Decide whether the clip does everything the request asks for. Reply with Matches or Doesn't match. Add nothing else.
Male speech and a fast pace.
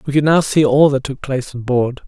Matches